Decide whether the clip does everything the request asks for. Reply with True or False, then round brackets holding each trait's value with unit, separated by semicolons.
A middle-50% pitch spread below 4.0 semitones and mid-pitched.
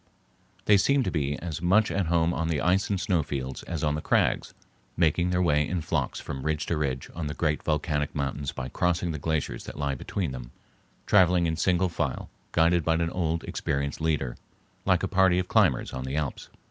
False (3.3 semitones; 80 Hz)